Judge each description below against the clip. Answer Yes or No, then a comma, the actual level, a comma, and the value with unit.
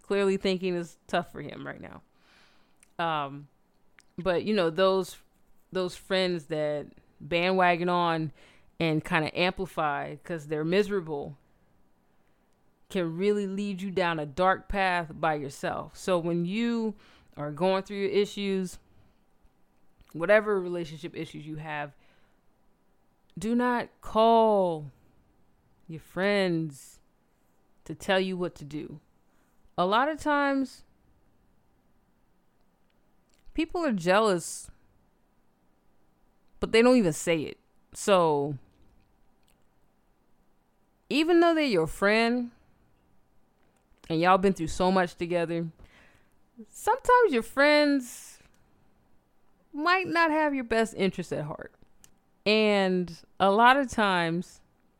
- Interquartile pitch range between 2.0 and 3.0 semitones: No, average, 4.6 semitones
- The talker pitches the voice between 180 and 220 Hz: Yes, medium, 185 Hz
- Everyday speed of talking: No, slow, 110 wpm